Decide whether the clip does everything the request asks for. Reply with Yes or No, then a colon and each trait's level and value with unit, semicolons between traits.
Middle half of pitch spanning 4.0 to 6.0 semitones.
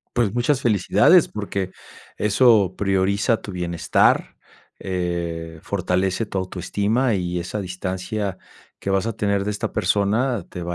No: average, 2.7 semitones